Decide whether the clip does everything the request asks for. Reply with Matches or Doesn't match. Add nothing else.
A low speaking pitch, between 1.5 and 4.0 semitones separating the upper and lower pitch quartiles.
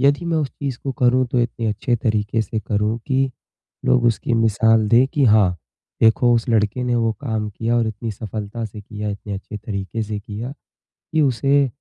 Matches